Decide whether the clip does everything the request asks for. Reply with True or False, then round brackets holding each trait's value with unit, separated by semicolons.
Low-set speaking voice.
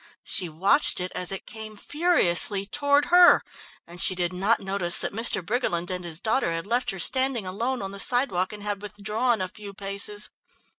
False (200 Hz)